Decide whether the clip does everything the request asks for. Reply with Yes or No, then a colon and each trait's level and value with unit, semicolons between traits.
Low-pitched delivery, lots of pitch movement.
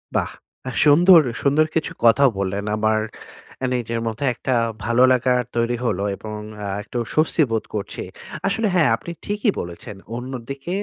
Yes: low, 125 Hz; wide, 5.7 semitones